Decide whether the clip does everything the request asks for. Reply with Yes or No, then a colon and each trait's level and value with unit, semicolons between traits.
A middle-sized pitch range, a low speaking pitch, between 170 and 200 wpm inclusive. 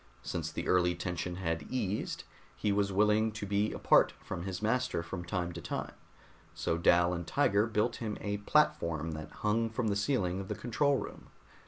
Yes: average, 3.9 semitones; low, 100 Hz; average, 185 wpm